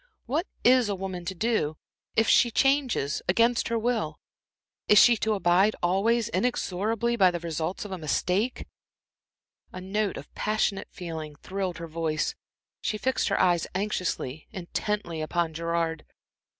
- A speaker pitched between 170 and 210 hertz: Yes, high, 190 Hz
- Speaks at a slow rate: No, average, 145 wpm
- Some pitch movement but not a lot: Yes, average, 4.8 semitones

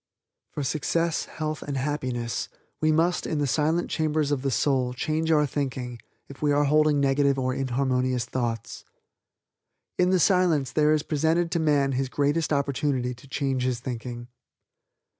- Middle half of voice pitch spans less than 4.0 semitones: Yes, average, 3.1 semitones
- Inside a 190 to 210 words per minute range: No, average, 160 wpm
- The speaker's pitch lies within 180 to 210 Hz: No, medium, 140 Hz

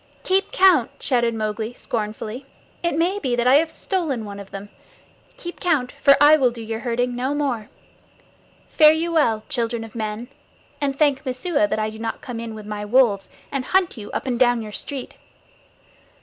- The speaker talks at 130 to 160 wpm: No, average, 190 wpm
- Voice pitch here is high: Yes, high, 245 Hz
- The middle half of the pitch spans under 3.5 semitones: No, average, 4.8 semitones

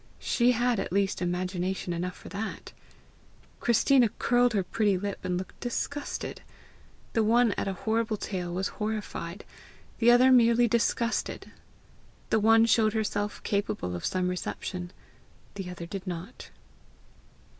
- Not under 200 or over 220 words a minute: No, slow, 135 wpm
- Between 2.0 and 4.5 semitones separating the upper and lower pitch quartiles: Yes, average, 4.1 semitones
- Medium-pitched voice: No, high, 205 Hz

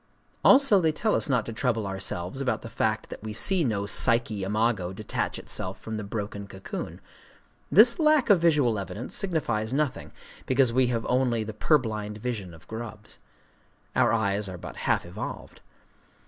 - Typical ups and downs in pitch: Yes, average, 4.2 semitones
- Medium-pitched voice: No, low, 115 Hz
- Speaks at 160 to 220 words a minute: Yes, average, 165 wpm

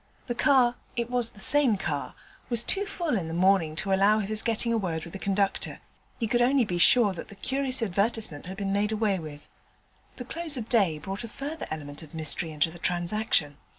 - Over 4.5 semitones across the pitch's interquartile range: Yes, wide, 5.6 semitones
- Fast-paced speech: Yes, fast, 220 wpm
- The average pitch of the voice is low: No, high, 205 Hz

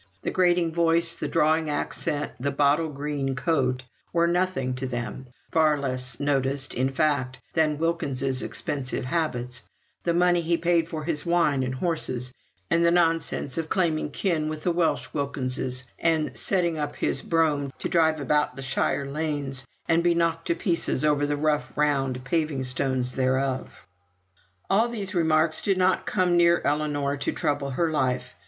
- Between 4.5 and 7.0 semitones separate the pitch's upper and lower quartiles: No, average, 3.8 semitones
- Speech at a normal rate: Yes, average, 160 wpm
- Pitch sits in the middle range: Yes, medium, 150 Hz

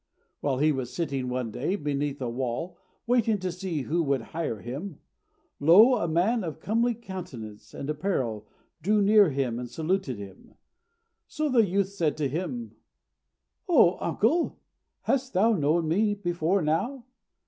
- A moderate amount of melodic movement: No, wide, 6.8 semitones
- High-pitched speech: No, medium, 170 Hz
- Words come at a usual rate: Yes, average, 155 wpm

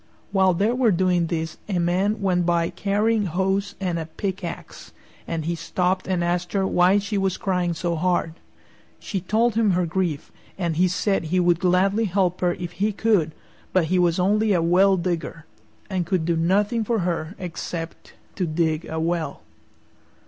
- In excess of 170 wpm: Yes, average, 180 wpm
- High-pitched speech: No, medium, 180 Hz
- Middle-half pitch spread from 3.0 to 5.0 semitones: No, narrow, 2.5 semitones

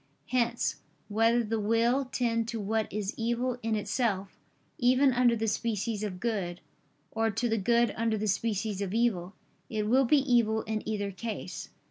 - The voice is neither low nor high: No, high, 225 Hz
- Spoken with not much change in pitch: Yes, narrow, 2.3 semitones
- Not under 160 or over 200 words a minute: Yes, average, 165 wpm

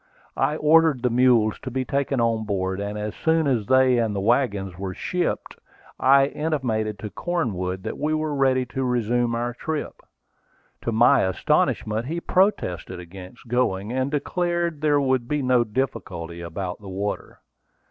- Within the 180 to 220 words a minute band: No, average, 160 wpm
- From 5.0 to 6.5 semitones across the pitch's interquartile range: Yes, wide, 5.4 semitones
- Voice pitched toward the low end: Yes, low, 120 Hz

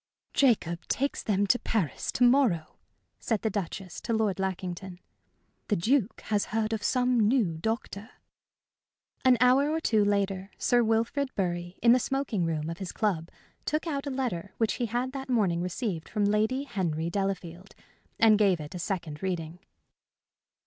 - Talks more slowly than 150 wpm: No, average, 165 wpm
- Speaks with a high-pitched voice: Yes, high, 205 Hz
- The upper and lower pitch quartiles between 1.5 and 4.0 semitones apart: No, wide, 5.4 semitones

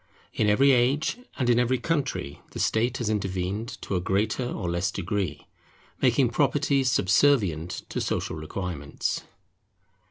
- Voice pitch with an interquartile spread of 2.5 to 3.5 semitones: No, wide, 5.6 semitones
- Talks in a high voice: No, low, 105 Hz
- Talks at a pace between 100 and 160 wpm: Yes, slow, 135 wpm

